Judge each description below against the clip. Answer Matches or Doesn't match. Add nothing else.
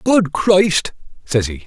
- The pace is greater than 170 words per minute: Doesn't match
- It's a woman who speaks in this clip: Doesn't match